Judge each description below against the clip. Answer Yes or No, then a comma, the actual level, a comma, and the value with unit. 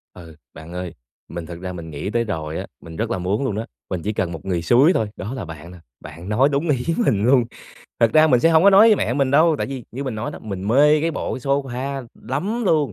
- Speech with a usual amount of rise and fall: No, wide, 7.6 semitones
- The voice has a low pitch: Yes, low, 120 Hz